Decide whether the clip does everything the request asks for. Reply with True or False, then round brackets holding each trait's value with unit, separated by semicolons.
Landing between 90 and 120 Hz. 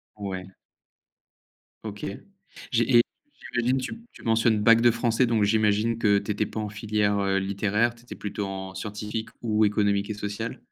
True (105 Hz)